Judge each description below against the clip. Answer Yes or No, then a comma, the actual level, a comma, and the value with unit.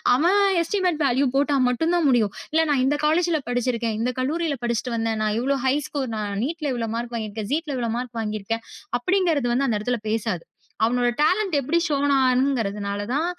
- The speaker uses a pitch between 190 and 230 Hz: No, very high, 250 Hz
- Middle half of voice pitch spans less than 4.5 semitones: No, average, 5.2 semitones